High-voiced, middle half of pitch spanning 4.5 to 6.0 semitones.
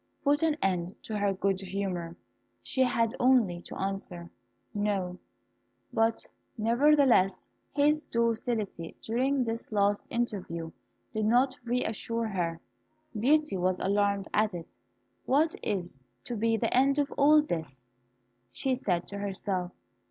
Yes: high, 210 Hz; average, 5.1 semitones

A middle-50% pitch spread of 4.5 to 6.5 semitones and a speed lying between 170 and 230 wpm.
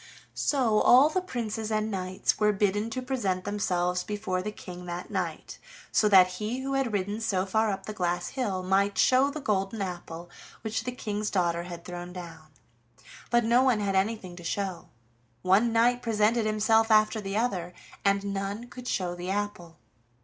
No: average, 3.5 semitones; average, 180 wpm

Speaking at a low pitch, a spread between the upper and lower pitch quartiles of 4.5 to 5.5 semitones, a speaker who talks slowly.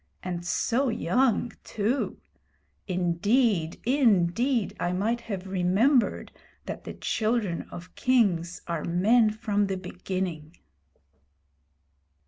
No: high, 200 Hz; average, 4.9 semitones; slow, 100 wpm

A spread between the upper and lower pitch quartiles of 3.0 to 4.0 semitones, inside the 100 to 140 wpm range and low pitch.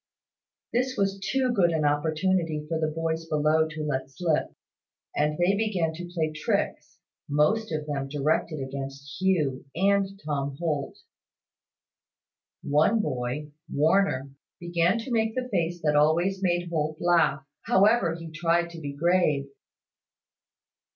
No: average, 3.6 semitones; slow, 135 wpm; medium, 160 Hz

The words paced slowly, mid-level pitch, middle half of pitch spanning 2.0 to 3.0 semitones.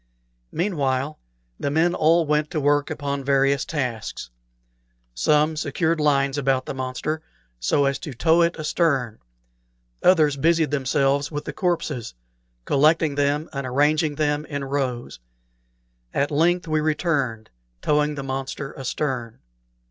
Yes: slow, 130 wpm; medium, 145 Hz; narrow, 2.4 semitones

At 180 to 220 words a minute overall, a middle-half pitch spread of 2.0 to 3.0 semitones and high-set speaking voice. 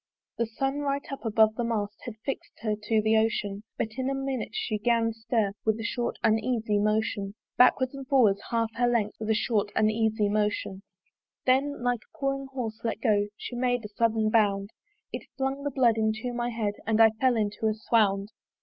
Yes: average, 195 wpm; narrow, 2.5 semitones; high, 225 Hz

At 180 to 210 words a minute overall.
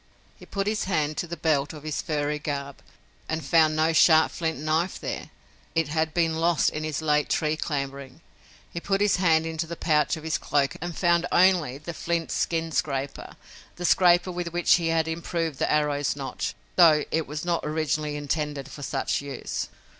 Yes: average, 190 wpm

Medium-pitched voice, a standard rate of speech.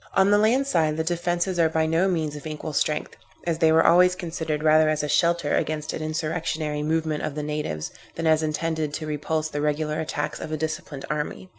No: medium, 155 Hz; fast, 210 wpm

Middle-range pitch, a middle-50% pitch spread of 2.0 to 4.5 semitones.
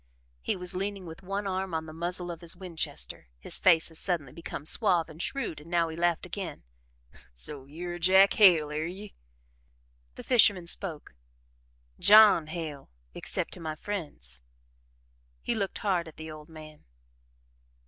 Yes: medium, 170 Hz; average, 3.2 semitones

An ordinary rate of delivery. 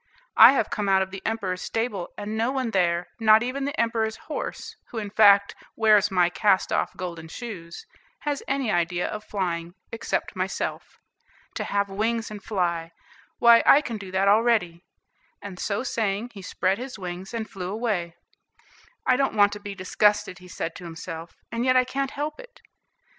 Yes: average, 180 wpm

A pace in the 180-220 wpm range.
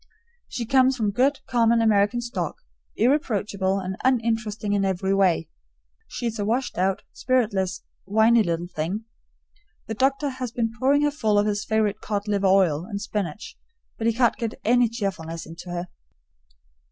No: average, 155 wpm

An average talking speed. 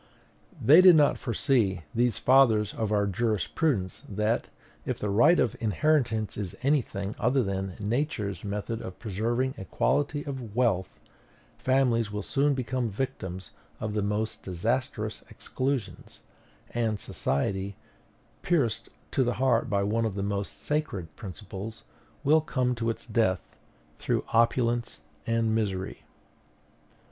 No: slow, 130 wpm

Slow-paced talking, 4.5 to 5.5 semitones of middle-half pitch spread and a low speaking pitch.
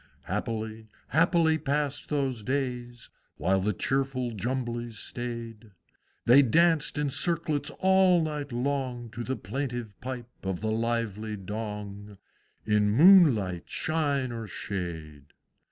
Yes: slow, 120 wpm; average, 4.9 semitones; low, 120 Hz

